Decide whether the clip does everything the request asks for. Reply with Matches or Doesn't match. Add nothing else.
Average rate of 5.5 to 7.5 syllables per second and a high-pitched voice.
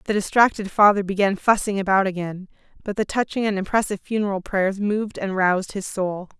Matches